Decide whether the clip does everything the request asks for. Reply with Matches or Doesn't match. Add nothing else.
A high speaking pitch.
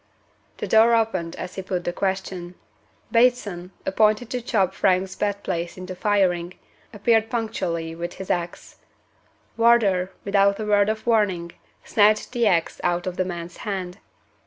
Matches